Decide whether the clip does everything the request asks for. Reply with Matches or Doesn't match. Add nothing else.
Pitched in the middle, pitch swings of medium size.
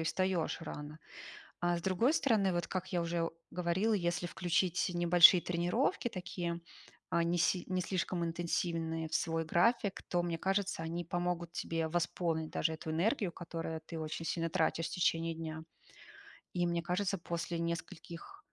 Doesn't match